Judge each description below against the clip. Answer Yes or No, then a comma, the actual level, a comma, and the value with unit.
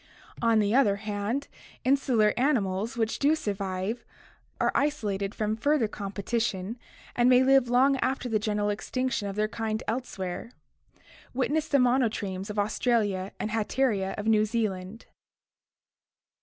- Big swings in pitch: No, average, 3.7 semitones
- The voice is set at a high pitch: Yes, high, 220 Hz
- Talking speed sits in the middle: No, slow, 130 wpm